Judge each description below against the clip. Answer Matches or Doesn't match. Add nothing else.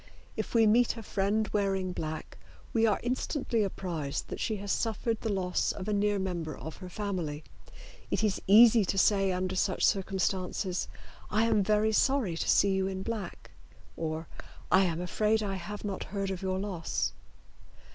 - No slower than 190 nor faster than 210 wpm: Doesn't match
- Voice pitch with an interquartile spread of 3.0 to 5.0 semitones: Doesn't match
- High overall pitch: Matches